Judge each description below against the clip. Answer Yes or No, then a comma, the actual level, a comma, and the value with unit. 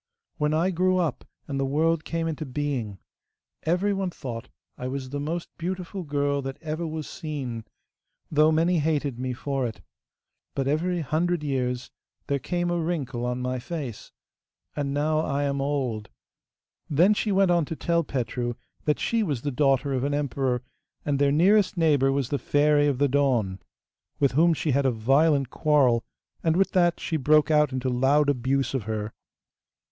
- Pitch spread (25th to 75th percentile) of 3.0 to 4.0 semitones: Yes, average, 3.7 semitones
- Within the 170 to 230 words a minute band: Yes, average, 175 wpm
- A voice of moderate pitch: Yes, medium, 145 Hz